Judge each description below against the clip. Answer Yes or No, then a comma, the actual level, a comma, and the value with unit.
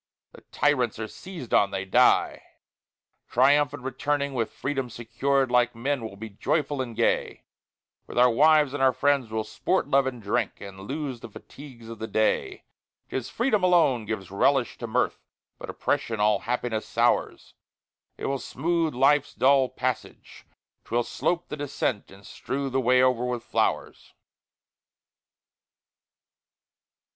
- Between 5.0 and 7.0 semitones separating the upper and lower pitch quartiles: No, average, 3.7 semitones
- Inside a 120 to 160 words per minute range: Yes, average, 150 wpm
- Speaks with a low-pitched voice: Yes, low, 130 Hz